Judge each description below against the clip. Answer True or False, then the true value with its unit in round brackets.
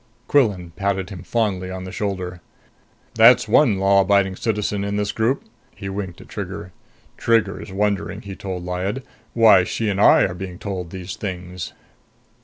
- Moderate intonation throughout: False (2.0 semitones)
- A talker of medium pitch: False (100 Hz)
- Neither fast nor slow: True (160 wpm)